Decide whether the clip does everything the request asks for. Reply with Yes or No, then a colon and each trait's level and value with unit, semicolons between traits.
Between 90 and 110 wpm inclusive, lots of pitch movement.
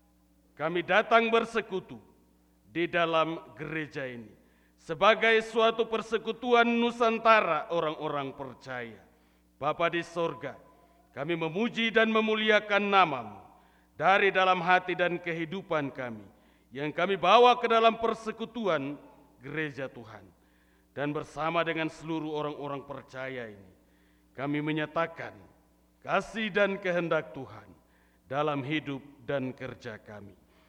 Yes: average, 105 wpm; wide, 7.7 semitones